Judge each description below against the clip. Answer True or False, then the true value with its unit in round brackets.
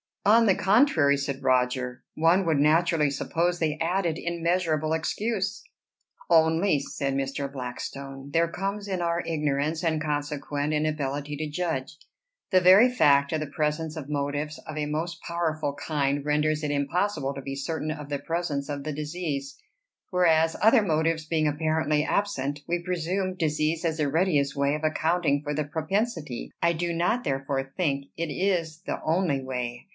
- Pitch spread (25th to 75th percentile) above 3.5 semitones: False (3.1 semitones)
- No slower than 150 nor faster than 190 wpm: True (160 wpm)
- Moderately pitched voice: True (155 Hz)